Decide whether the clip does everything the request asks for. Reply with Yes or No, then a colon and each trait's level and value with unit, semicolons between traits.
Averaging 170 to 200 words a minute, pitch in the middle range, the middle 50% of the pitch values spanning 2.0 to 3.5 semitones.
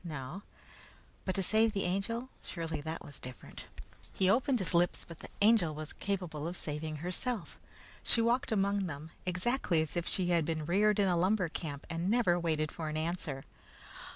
No: average, 180 wpm; medium, 175 Hz; average, 4.1 semitones